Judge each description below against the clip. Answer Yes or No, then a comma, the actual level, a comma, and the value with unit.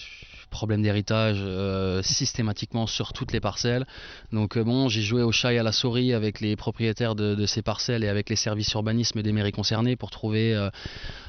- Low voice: Yes, low, 110 Hz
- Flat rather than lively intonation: Yes, narrow, 2.1 semitones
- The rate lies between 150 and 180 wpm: No, average, 195 wpm